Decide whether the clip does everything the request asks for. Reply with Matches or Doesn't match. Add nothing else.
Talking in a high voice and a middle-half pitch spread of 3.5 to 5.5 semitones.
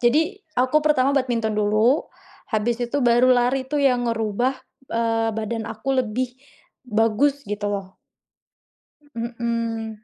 Doesn't match